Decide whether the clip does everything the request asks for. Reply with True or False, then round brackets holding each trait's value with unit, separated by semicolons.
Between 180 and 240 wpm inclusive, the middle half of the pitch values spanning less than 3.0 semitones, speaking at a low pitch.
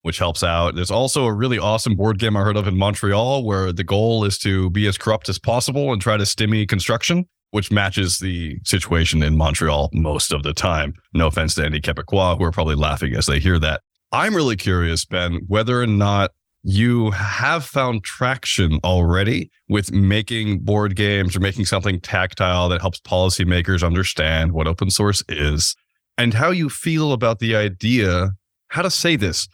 False (185 wpm; 3.7 semitones; 100 Hz)